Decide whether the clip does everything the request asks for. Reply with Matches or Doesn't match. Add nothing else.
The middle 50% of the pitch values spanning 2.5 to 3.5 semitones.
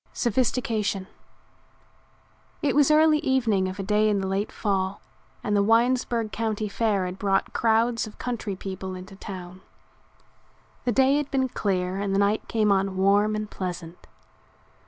Matches